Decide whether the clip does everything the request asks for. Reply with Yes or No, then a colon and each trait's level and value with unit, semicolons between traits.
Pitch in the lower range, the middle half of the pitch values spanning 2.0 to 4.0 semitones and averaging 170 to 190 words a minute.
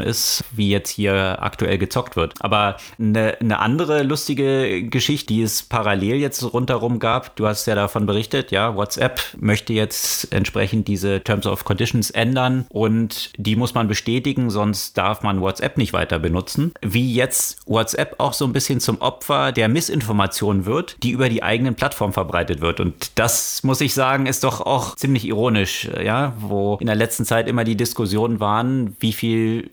Yes: low, 115 Hz; average, 3.6 semitones; average, 175 wpm